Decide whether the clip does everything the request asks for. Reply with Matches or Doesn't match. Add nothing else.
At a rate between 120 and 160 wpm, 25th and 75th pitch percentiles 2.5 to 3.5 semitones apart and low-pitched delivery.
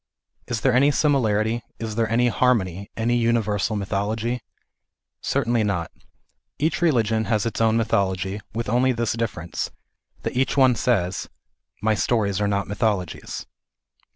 Matches